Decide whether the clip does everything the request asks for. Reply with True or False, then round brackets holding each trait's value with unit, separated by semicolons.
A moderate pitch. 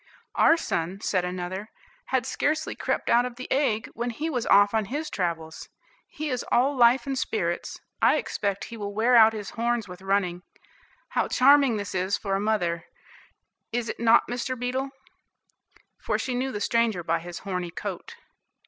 False (225 Hz)